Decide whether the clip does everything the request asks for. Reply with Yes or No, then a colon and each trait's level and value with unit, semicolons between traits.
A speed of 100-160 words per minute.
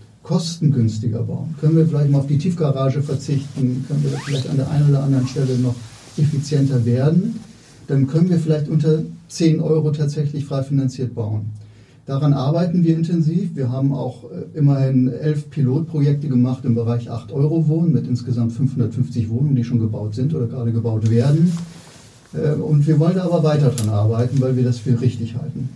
No: average, 170 wpm